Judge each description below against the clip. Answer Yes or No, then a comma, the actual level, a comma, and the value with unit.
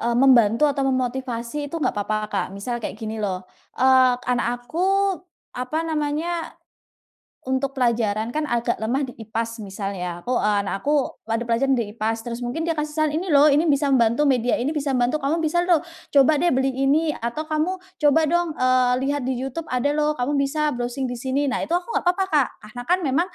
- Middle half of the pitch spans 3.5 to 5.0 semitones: Yes, average, 4.3 semitones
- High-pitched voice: Yes, very high, 265 Hz